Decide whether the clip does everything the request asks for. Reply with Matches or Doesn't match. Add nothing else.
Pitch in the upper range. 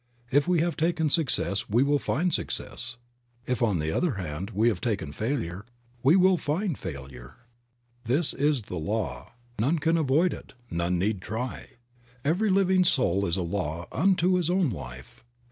Doesn't match